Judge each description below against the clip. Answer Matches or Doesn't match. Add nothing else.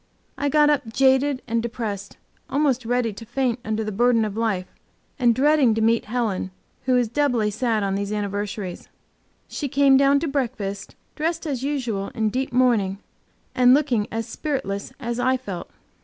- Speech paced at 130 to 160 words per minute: Doesn't match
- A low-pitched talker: Doesn't match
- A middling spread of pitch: Matches